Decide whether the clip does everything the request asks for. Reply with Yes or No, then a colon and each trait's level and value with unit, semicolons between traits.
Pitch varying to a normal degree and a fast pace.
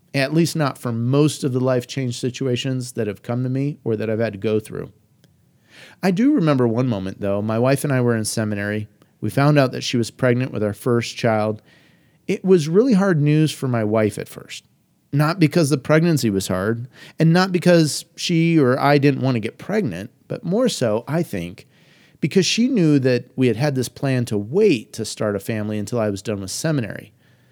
No: wide, 5.7 semitones; fast, 215 wpm